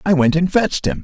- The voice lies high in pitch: No, medium, 150 Hz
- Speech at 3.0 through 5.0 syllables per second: No, 6.5 syllables/s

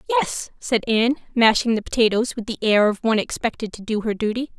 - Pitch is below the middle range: No, high, 230 Hz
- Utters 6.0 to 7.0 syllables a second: Yes, 6.1 syllables/s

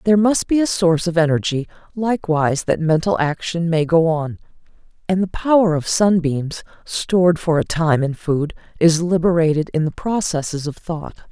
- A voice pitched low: No, medium, 170 Hz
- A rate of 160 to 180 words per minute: Yes, average, 170 wpm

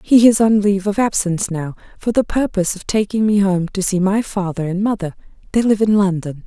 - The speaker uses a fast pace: Yes, fast, 215 wpm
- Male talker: No, female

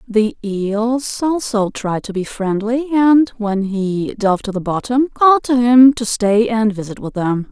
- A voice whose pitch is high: Yes, high, 225 Hz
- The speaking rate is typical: Yes, average, 185 wpm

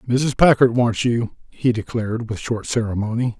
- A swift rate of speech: No, average, 160 wpm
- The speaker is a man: Yes, male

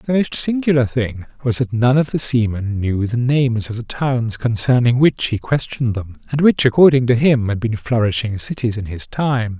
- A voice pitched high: No, low, 120 Hz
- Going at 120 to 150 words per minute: No, fast, 205 wpm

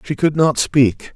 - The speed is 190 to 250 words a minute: Yes, fast, 210 wpm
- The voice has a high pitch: No, medium, 140 Hz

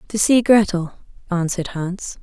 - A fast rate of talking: No, slow, 135 wpm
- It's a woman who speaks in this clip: Yes, female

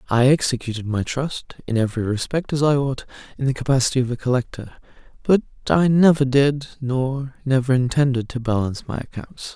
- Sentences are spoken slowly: No, average, 170 wpm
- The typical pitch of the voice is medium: No, low, 130 Hz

